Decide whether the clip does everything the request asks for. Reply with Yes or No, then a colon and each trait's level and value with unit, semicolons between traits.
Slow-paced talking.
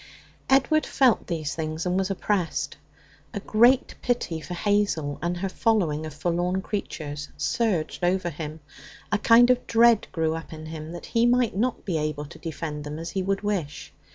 No: average, 180 wpm